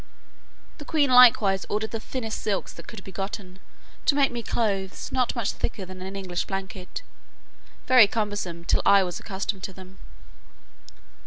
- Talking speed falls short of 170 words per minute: Yes, average, 160 wpm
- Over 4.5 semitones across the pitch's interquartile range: No, average, 3.3 semitones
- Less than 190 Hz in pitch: No, high, 200 Hz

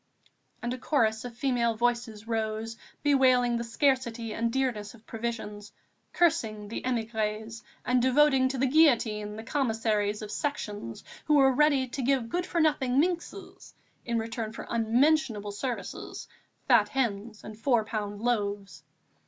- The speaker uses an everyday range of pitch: Yes, average, 3.4 semitones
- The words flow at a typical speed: Yes, average, 145 wpm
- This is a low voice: No, high, 235 Hz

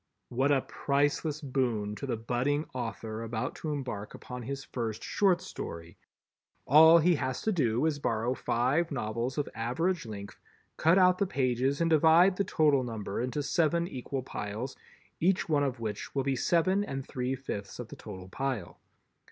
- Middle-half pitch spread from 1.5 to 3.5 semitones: No, average, 5.1 semitones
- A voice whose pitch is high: No, low, 135 Hz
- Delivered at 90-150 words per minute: No, average, 175 wpm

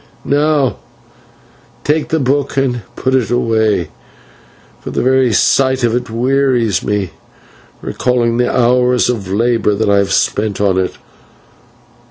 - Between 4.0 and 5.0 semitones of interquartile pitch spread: No, average, 3.4 semitones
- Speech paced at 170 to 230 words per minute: No, slow, 135 wpm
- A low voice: Yes, low, 120 Hz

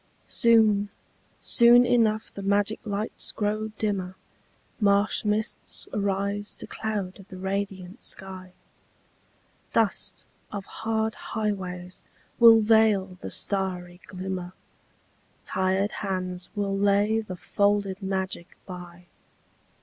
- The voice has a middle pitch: No, high, 200 Hz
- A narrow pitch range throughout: Yes, narrow, 2.2 semitones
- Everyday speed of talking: No, slow, 100 wpm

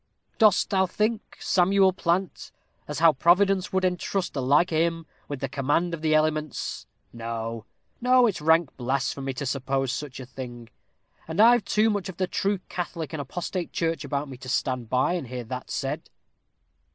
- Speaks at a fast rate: No, average, 175 wpm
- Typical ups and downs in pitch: No, wide, 5.8 semitones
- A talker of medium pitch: Yes, medium, 160 Hz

